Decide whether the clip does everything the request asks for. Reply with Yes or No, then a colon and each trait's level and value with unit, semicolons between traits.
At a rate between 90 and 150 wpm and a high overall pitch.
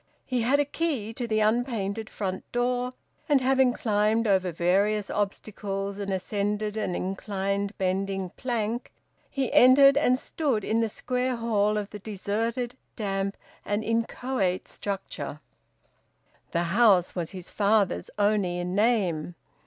Yes: slow, 135 wpm; high, 210 Hz